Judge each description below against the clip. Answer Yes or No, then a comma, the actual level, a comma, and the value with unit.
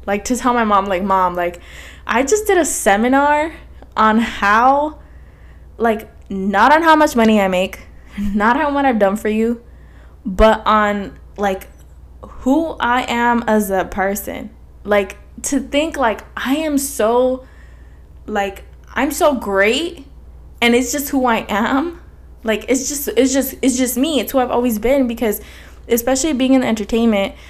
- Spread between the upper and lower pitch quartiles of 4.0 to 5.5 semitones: Yes, average, 4.7 semitones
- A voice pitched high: Yes, high, 235 Hz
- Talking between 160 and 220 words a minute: Yes, average, 165 wpm